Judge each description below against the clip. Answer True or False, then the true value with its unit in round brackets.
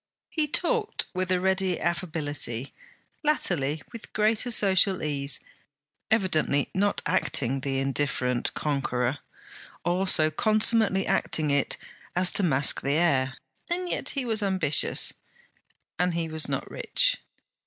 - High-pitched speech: False (175 Hz)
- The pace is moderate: False (125 wpm)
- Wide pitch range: True (6.3 semitones)